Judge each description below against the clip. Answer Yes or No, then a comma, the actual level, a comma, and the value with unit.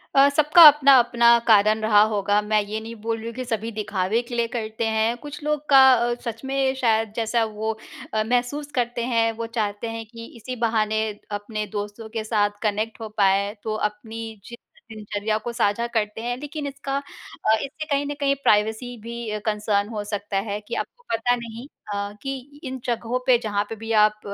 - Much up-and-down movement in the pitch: No, narrow, 2.4 semitones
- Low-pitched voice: No, high, 225 Hz